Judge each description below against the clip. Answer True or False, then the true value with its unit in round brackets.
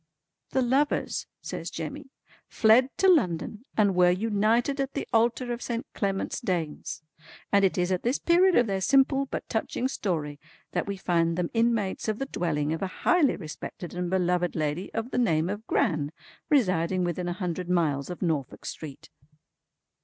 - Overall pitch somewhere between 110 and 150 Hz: False (190 Hz)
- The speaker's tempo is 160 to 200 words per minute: True (170 wpm)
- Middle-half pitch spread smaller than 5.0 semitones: False (5.6 semitones)